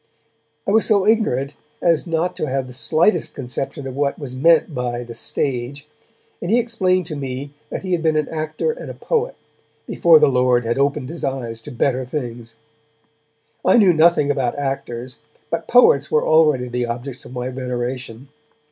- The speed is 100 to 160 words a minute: No, average, 180 wpm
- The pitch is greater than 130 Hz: Yes, medium, 140 Hz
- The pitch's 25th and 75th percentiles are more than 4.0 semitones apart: Yes, average, 4.7 semitones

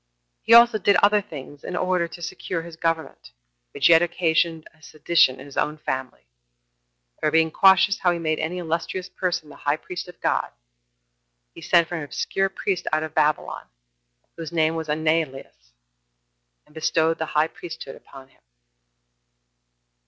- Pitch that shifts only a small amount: Yes, narrow, 2.3 semitones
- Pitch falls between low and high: Yes, medium, 165 Hz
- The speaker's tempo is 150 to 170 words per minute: Yes, average, 165 wpm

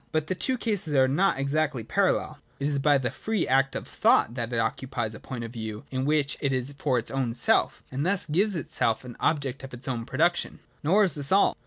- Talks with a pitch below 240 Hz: Yes, medium, 140 Hz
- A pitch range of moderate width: Yes, average, 4.0 semitones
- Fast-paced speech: Yes, fast, 230 wpm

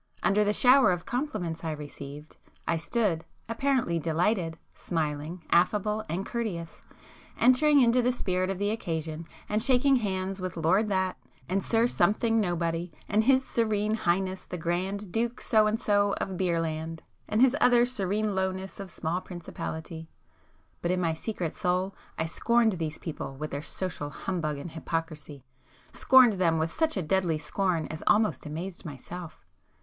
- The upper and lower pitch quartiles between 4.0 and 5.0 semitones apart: Yes, average, 4.7 semitones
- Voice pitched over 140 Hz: Yes, medium, 185 Hz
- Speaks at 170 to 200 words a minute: No, average, 155 wpm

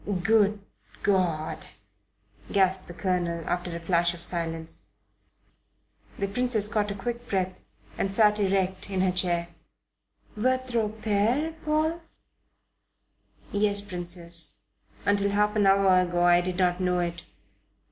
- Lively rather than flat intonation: No, average, 3.0 semitones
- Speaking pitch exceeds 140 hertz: Yes, high, 190 Hz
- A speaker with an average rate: No, slow, 125 wpm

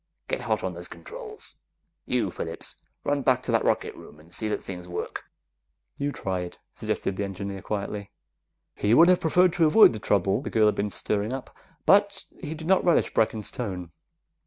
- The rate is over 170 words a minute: Yes, average, 190 wpm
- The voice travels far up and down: Yes, wide, 8.4 semitones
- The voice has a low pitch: Yes, low, 110 Hz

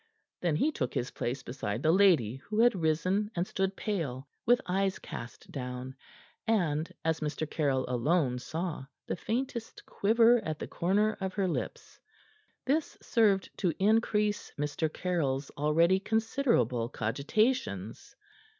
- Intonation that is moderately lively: No, wide, 7.2 semitones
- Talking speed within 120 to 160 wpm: Yes, slow, 135 wpm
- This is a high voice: No, medium, 170 Hz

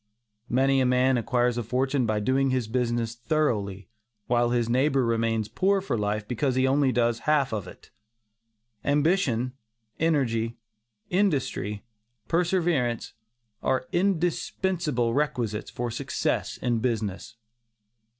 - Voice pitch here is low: Yes, low, 125 Hz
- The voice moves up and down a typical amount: Yes, average, 4.0 semitones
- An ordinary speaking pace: No, slow, 115 wpm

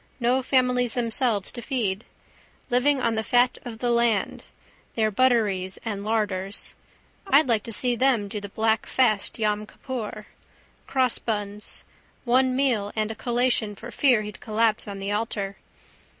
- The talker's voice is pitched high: Yes, high, 225 Hz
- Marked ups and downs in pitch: No, average, 3.0 semitones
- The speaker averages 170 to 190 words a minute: No, average, 150 wpm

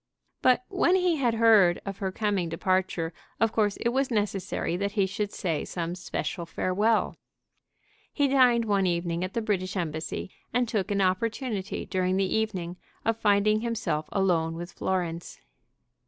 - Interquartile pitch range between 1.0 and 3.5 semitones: No, average, 3.9 semitones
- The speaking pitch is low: No, high, 195 Hz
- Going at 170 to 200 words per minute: No, average, 155 wpm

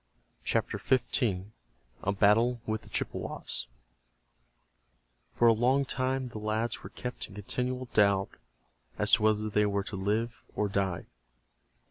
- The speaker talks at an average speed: No, slow, 130 wpm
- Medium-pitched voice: No, low, 110 Hz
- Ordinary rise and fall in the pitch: Yes, average, 3.2 semitones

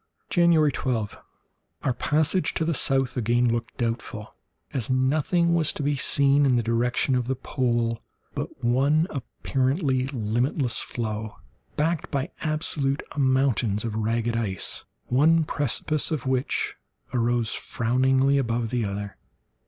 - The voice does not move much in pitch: No, average, 3.4 semitones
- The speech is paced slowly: Yes, slow, 130 wpm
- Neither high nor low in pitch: No, low, 130 Hz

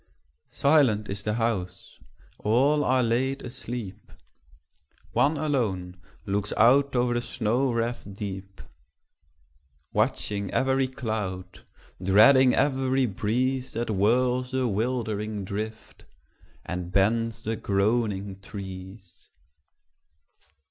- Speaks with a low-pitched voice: Yes, low, 110 Hz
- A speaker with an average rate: No, slow, 95 wpm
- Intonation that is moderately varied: Yes, average, 4.4 semitones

